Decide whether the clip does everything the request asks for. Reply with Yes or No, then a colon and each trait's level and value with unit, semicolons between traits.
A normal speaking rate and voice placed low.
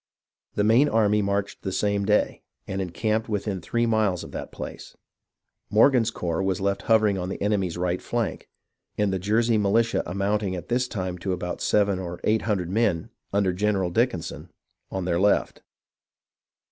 Yes: average, 165 wpm; low, 100 Hz